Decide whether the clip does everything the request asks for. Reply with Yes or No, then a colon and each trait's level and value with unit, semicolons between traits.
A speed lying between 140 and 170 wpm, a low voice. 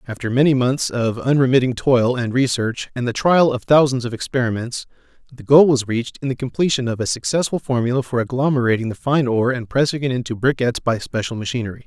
No: average, 195 wpm; low, 125 Hz